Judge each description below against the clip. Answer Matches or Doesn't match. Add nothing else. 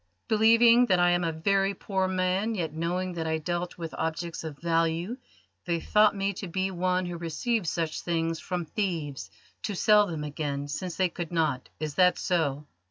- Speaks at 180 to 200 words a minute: Matches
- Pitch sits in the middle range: Matches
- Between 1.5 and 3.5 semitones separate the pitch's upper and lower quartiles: Matches